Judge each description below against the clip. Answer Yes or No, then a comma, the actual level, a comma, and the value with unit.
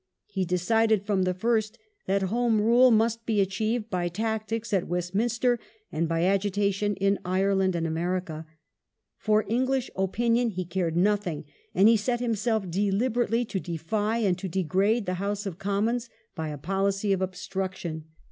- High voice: Yes, high, 200 Hz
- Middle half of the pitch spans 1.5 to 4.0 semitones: Yes, average, 3.4 semitones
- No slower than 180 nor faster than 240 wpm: No, average, 155 wpm